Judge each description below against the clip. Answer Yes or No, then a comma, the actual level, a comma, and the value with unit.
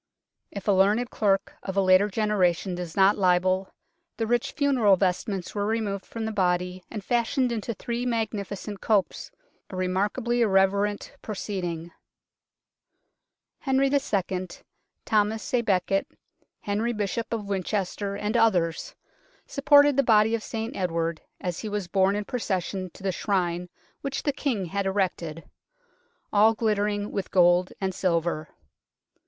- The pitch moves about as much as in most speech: Yes, average, 3.2 semitones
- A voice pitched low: No, high, 200 Hz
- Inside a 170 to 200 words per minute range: No, average, 145 wpm